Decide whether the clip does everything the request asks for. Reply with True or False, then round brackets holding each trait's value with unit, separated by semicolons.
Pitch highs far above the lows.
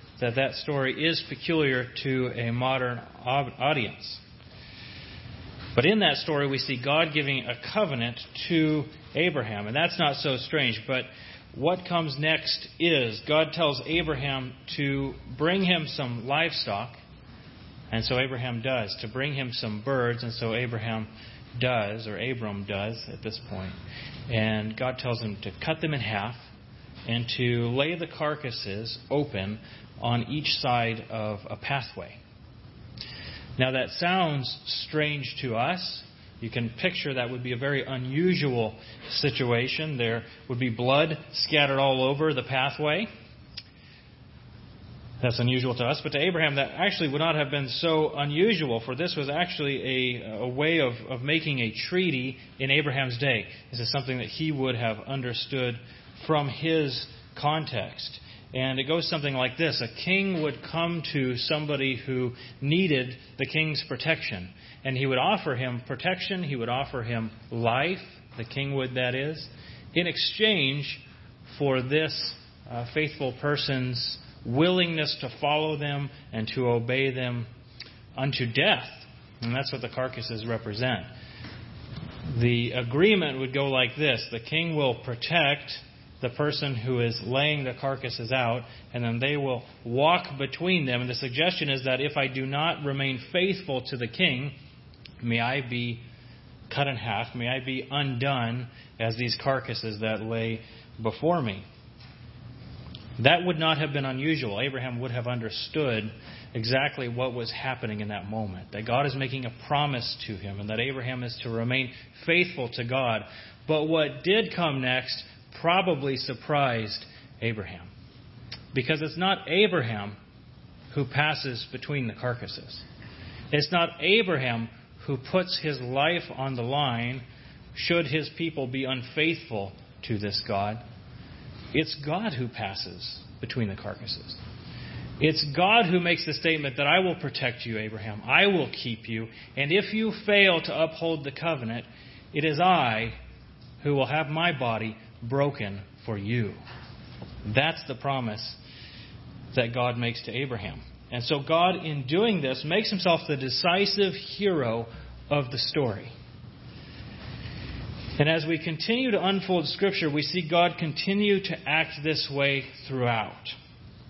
False (4.2 semitones)